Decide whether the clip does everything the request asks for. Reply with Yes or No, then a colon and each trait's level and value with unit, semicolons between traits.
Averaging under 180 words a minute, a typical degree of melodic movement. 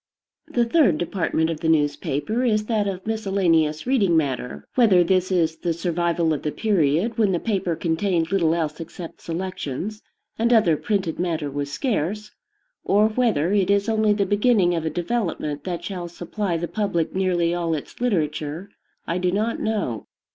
Yes: average, 170 wpm; average, 4.4 semitones